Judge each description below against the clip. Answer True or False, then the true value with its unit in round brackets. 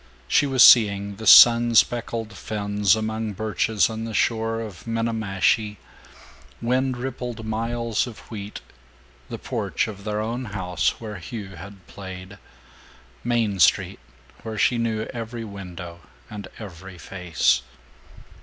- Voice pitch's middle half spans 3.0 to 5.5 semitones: False (2.6 semitones)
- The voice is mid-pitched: False (110 Hz)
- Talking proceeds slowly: True (125 wpm)